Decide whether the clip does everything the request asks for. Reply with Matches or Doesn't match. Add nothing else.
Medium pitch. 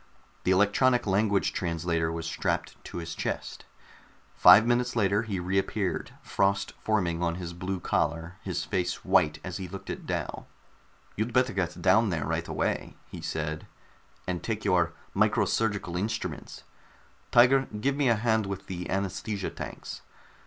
Doesn't match